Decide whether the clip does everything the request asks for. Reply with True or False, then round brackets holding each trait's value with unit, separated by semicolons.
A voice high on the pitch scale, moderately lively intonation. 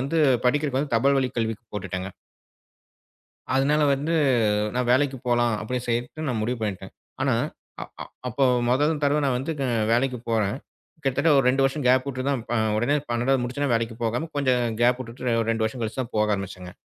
False (125 Hz; 3.0 semitones)